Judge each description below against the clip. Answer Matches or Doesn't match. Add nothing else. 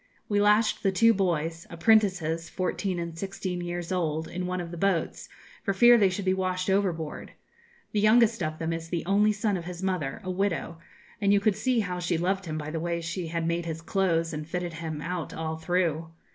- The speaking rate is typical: Doesn't match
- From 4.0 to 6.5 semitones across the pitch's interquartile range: Doesn't match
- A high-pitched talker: Doesn't match